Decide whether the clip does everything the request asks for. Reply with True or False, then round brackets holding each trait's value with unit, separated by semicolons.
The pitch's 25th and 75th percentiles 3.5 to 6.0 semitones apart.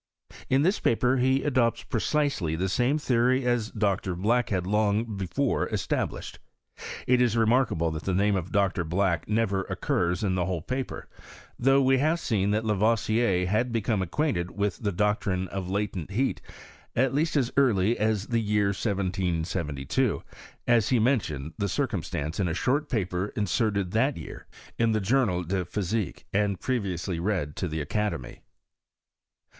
True (4.8 semitones)